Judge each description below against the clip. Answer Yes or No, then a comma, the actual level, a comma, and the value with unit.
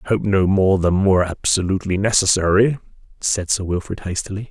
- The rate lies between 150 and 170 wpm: Yes, average, 160 wpm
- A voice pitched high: No, very low, 95 Hz